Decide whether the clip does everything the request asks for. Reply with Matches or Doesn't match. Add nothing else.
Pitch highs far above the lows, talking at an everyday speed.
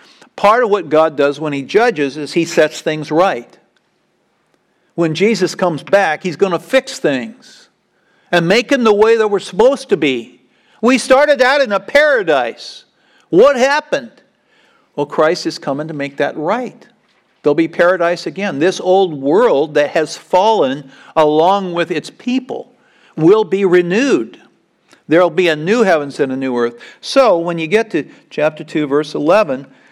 Matches